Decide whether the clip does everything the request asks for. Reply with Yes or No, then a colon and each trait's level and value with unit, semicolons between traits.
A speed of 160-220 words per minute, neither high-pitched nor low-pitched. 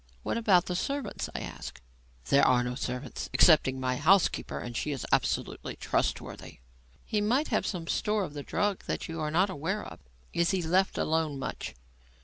Yes: average, 180 wpm; medium, 165 Hz